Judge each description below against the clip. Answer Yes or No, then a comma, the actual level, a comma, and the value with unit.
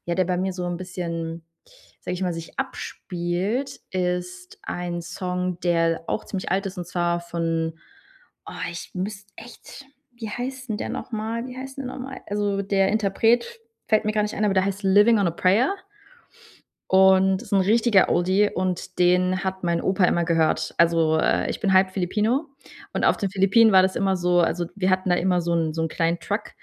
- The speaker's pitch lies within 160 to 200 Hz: Yes, medium, 185 Hz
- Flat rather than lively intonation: No, average, 3.0 semitones